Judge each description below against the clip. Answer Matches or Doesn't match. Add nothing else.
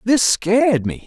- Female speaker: Doesn't match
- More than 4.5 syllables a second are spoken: Doesn't match